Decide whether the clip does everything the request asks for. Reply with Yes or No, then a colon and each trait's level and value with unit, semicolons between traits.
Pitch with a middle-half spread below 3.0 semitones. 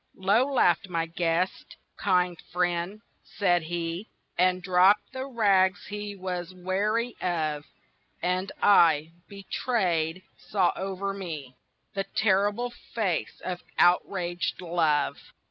Yes: narrow, 2.6 semitones